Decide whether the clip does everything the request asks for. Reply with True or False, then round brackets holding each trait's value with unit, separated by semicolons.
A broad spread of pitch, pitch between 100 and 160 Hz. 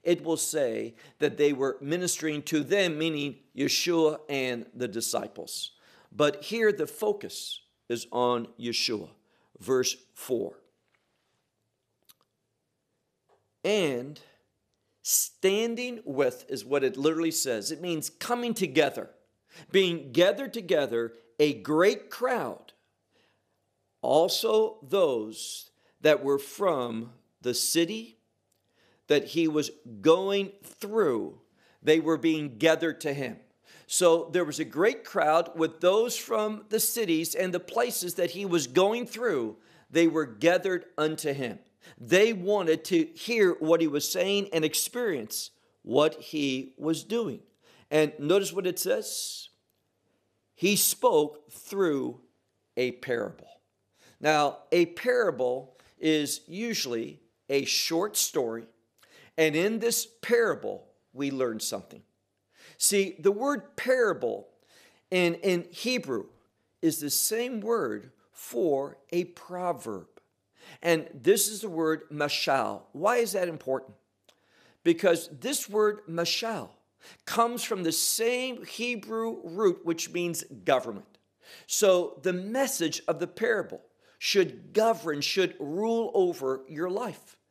False (6.6 semitones; 170 Hz)